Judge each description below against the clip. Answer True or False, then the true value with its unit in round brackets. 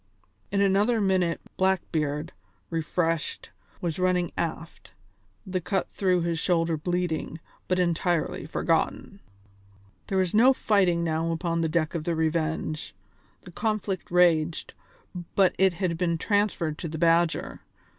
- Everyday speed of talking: False (130 wpm)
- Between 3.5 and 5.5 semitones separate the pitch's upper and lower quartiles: False (2.4 semitones)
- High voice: False (170 Hz)